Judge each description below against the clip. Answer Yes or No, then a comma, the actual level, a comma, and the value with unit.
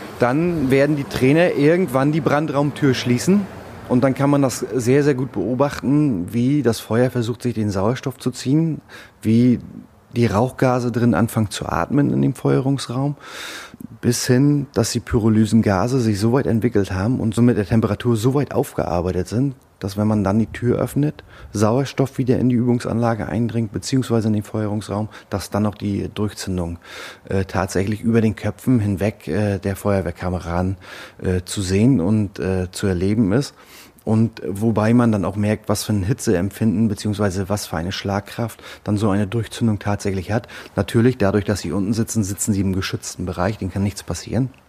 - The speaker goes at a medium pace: Yes, average, 175 wpm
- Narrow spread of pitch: No, average, 3.8 semitones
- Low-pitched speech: Yes, low, 115 Hz